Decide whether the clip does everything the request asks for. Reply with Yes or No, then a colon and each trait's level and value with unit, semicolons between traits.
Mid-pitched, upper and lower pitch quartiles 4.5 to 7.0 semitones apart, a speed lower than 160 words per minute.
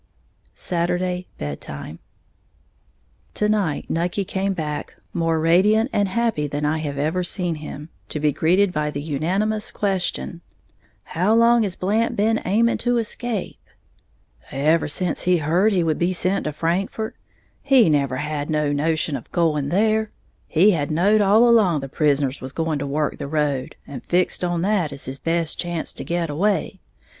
No: medium, 170 Hz; average, 5.0 semitones; average, 165 wpm